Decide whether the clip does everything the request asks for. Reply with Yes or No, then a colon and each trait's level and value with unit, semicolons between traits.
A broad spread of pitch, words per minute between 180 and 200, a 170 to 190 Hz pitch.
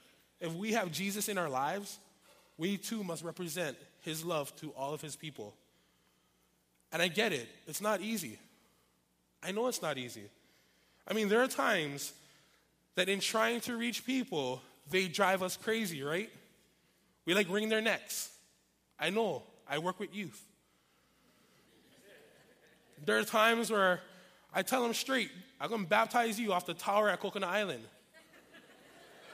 No: wide, 6.8 semitones; average, 155 wpm; medium, 185 Hz